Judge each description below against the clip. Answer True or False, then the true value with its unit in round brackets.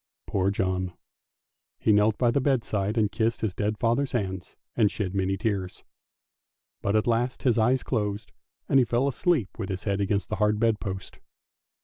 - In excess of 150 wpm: True (175 wpm)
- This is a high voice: False (105 Hz)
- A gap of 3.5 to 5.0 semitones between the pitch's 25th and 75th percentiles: False (3.1 semitones)